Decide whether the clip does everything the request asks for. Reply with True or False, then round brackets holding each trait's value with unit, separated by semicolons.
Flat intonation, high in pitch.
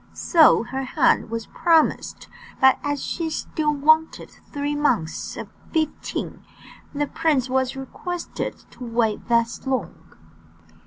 False (4.1 semitones; 280 Hz)